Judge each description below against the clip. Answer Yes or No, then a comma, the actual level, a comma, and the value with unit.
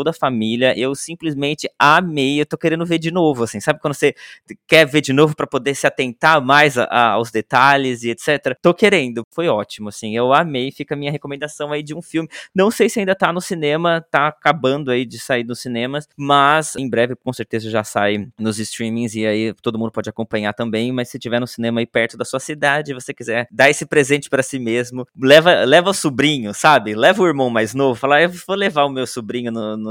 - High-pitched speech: No, low, 135 Hz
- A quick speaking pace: Yes, fast, 225 wpm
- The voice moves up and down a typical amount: Yes, average, 4.6 semitones